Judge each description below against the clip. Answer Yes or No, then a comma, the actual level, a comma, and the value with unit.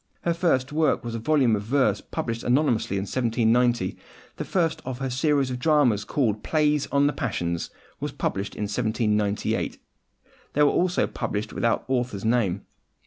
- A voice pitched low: Yes, low, 125 Hz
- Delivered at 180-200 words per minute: No, average, 165 wpm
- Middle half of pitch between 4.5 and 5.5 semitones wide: Yes, average, 5.1 semitones